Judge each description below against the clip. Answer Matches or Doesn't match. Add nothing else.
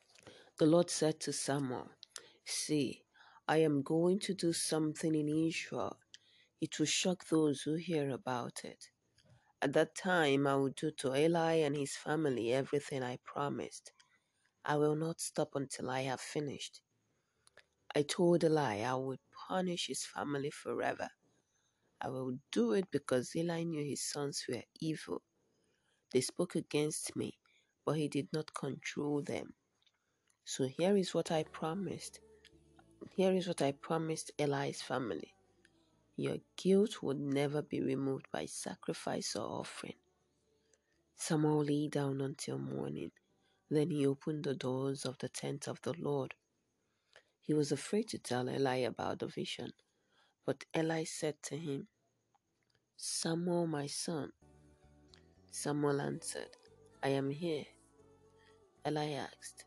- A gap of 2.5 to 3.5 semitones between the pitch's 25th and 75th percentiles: Matches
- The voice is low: Doesn't match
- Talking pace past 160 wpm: Doesn't match